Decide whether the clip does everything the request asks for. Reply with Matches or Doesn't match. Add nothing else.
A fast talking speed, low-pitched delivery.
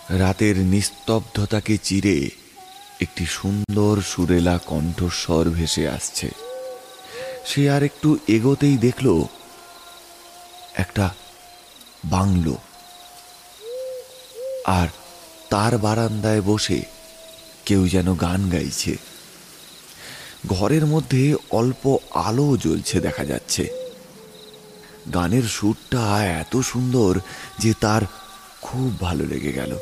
Doesn't match